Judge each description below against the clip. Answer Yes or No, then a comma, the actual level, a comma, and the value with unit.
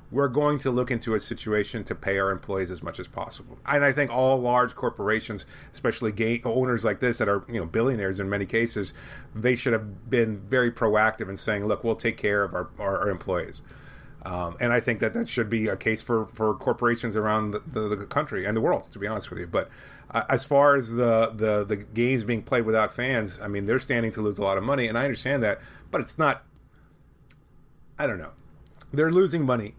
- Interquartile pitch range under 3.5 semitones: Yes, average, 3.1 semitones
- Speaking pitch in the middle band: No, low, 115 Hz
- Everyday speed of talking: No, fast, 230 wpm